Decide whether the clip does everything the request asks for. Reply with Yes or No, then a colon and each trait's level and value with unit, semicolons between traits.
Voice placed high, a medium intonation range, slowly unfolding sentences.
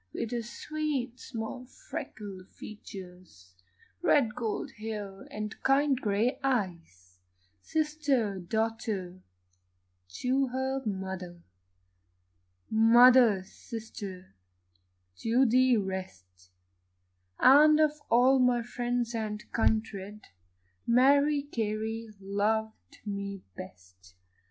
Yes: high, 220 Hz; average, 4.7 semitones; slow, 85 wpm